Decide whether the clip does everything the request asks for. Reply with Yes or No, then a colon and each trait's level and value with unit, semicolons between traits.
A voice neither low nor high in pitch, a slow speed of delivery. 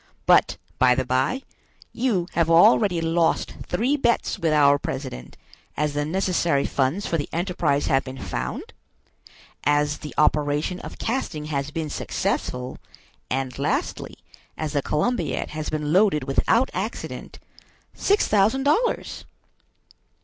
Yes: medium, 155 Hz; slow, 130 wpm